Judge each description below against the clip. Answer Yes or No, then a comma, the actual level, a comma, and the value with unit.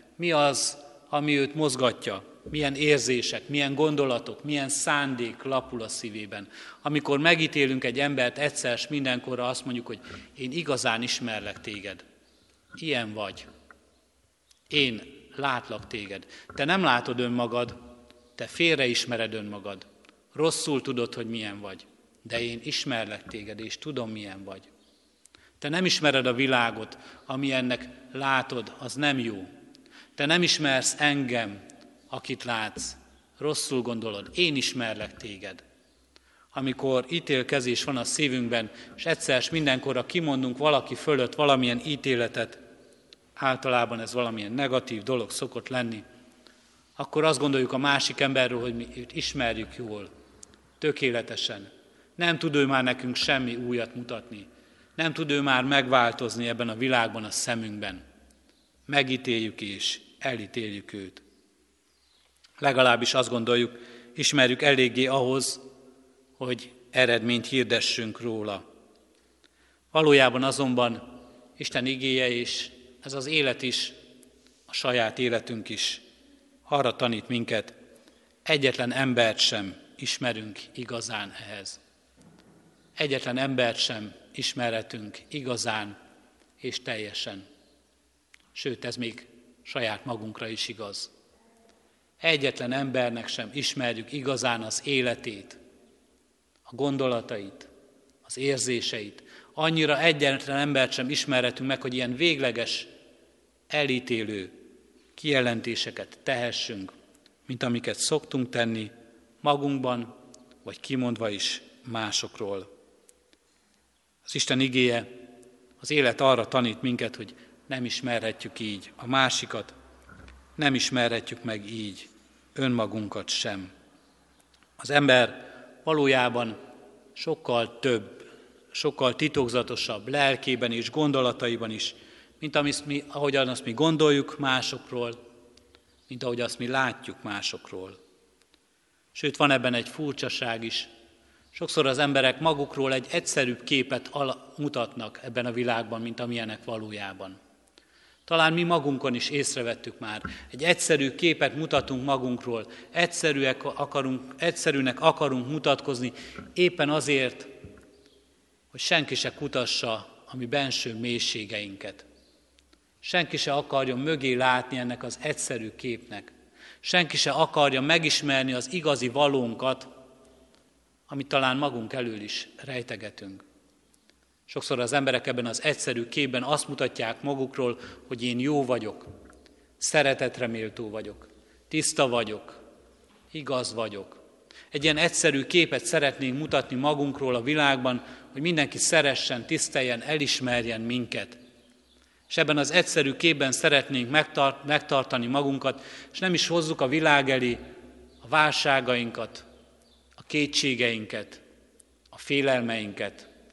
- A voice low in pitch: Yes, low, 125 Hz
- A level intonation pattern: No, average, 3.1 semitones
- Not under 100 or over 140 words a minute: Yes, average, 110 wpm